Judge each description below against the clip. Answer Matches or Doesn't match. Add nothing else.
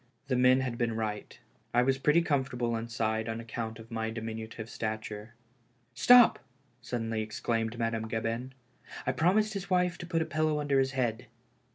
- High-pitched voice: Doesn't match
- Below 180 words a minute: Doesn't match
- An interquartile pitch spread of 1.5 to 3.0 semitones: Doesn't match